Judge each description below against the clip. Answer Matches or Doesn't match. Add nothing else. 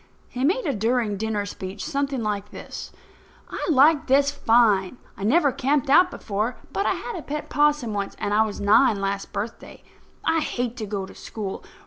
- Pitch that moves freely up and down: Matches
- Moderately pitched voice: Doesn't match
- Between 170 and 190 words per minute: Matches